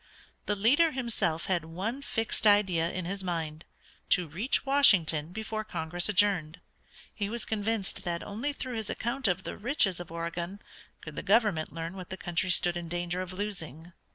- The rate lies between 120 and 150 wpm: No, average, 175 wpm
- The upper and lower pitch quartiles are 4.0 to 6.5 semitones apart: Yes, average, 4.4 semitones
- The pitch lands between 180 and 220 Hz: Yes, medium, 185 Hz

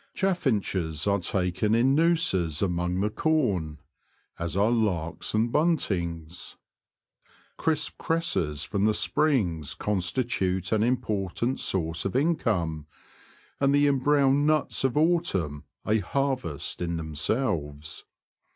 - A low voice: Yes, low, 105 Hz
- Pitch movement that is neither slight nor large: No, wide, 8.1 semitones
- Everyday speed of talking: No, slow, 110 wpm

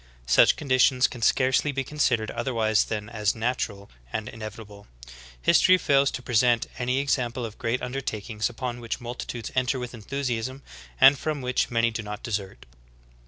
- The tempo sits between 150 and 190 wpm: Yes, average, 160 wpm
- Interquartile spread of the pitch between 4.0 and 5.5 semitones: No, average, 2.8 semitones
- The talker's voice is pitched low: Yes, low, 120 Hz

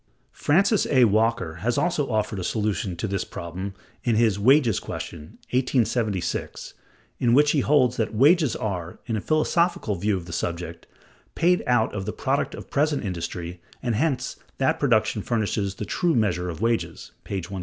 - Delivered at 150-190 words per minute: Yes, average, 170 wpm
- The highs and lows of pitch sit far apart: Yes, wide, 5.8 semitones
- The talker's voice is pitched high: No, low, 110 Hz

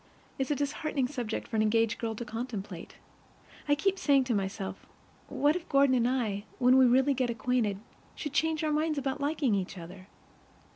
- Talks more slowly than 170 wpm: No, average, 185 wpm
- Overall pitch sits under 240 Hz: No, very high, 255 Hz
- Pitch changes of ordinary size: Yes, average, 4.5 semitones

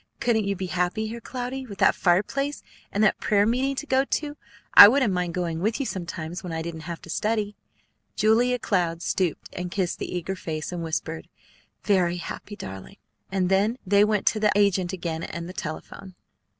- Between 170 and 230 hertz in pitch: Yes, high, 190 Hz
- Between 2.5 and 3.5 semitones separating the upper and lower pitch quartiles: No, average, 3.9 semitones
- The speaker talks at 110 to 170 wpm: No, average, 190 wpm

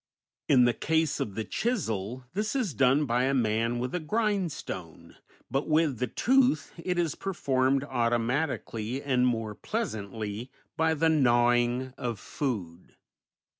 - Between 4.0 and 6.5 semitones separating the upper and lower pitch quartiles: Yes, wide, 5.5 semitones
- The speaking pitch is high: No, low, 130 Hz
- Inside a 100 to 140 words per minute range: Yes, slow, 135 wpm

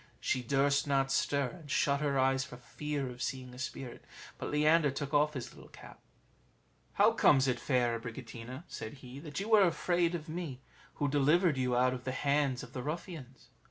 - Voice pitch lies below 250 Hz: Yes, medium, 140 Hz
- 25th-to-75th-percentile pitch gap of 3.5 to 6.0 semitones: No, average, 2.7 semitones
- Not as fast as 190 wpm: No, average, 195 wpm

